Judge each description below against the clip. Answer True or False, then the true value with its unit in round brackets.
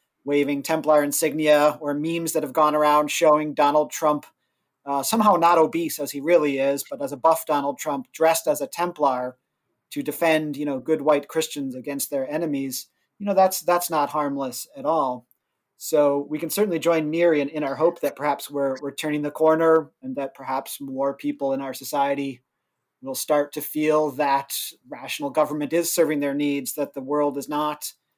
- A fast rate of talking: False (185 wpm)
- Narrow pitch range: True (2.1 semitones)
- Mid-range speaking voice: True (150 Hz)